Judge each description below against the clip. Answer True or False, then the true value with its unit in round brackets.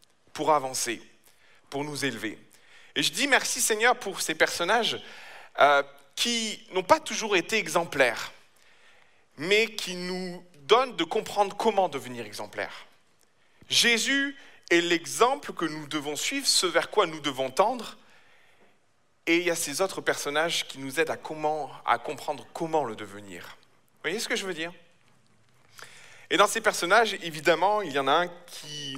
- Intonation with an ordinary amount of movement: False (6.1 semitones)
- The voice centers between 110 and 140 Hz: False (170 Hz)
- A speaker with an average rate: True (160 wpm)